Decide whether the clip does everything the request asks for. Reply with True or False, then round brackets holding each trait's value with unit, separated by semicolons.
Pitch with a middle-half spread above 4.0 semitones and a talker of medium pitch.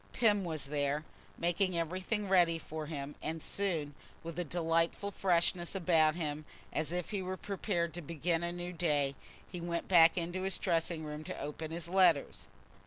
False (2.5 semitones; 170 Hz)